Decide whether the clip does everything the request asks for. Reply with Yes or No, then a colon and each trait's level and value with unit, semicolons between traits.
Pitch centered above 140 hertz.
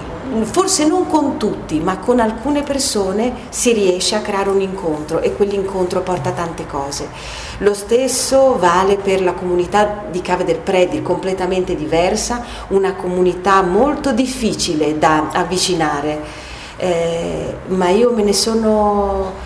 Yes: high, 190 Hz